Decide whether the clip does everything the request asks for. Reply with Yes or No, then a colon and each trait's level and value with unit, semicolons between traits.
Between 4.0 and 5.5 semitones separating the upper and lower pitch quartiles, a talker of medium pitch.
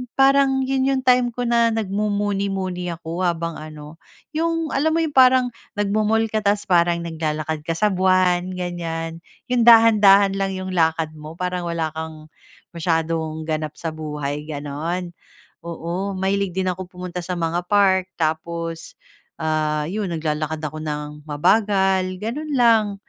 Yes: average, 4.5 semitones; medium, 180 Hz